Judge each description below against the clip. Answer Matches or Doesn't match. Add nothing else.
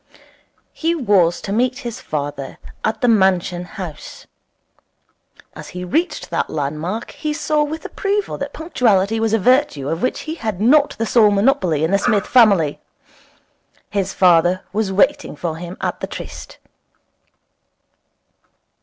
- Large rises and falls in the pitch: Matches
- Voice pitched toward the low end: Doesn't match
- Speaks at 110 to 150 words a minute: Matches